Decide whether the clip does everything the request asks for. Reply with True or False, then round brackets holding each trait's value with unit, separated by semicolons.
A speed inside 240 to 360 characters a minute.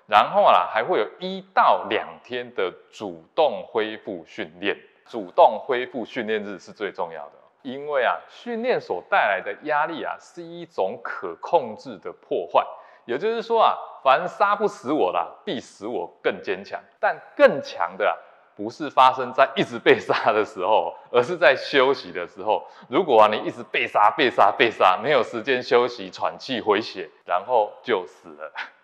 True (245 characters per minute)